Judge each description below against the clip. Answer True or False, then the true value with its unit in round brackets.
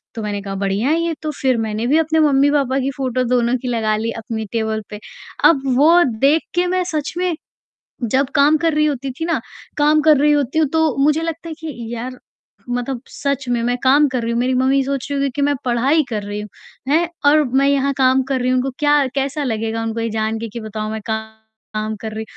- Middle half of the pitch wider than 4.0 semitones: True (4.6 semitones)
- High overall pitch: True (265 Hz)